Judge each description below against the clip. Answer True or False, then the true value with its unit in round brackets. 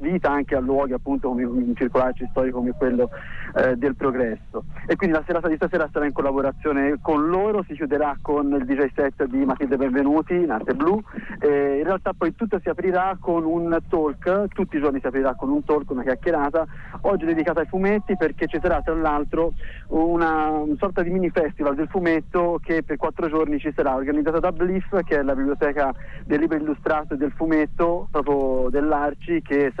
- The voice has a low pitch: False (150 Hz)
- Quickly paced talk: True (195 wpm)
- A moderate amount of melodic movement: True (3.3 semitones)